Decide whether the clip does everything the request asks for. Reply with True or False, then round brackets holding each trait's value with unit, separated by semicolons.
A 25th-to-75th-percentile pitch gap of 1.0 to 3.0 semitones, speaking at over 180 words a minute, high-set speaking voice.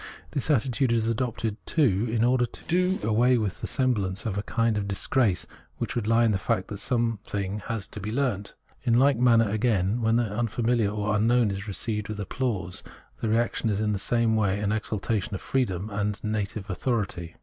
False (2.7 semitones; 205 wpm; 110 Hz)